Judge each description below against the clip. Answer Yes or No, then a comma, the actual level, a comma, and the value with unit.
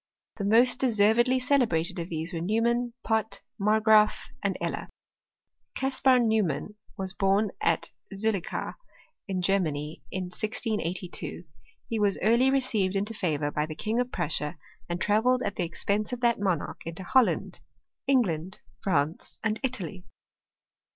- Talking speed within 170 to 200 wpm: No, slow, 135 wpm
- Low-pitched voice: No, high, 205 Hz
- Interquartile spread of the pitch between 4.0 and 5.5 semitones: Yes, average, 4.6 semitones